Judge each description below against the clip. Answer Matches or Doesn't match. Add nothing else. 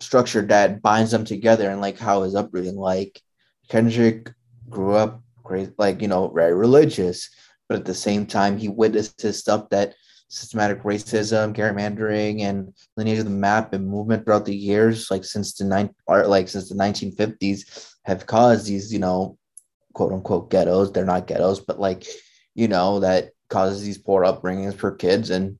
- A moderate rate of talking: Matches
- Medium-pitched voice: Doesn't match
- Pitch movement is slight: Matches